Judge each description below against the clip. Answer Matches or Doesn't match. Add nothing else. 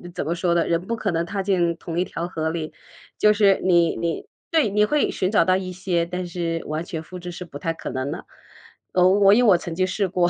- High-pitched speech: Doesn't match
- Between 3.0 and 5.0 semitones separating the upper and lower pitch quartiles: Doesn't match